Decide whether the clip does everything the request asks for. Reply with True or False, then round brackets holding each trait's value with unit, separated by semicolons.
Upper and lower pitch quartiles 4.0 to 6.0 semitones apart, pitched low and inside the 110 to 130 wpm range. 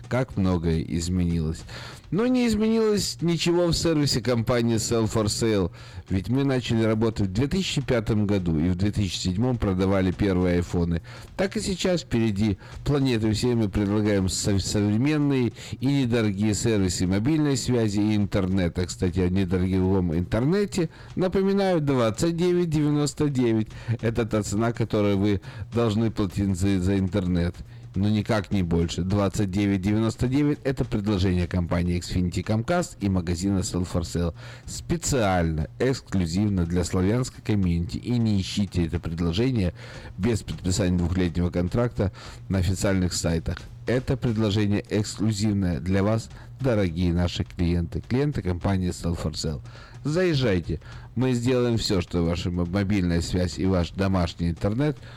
True (5.0 semitones; 105 Hz; 125 wpm)